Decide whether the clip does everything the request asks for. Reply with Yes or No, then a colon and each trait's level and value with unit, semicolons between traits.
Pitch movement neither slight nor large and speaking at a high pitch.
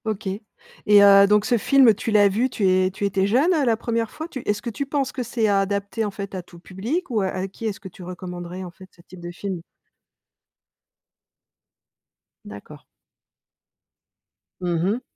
Yes: average, 3.5 semitones; high, 200 Hz